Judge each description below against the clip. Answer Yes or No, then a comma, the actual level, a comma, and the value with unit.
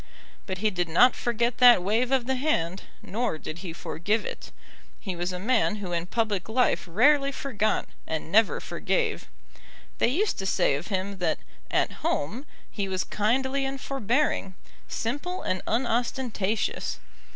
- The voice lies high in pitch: Yes, high, 220 Hz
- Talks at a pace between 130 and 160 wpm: Yes, average, 155 wpm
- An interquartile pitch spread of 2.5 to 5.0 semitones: No, wide, 5.5 semitones